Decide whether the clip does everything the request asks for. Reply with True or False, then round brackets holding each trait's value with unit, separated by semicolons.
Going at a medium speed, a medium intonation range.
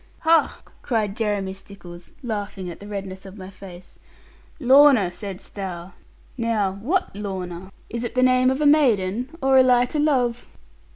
True (160 wpm; 4.9 semitones)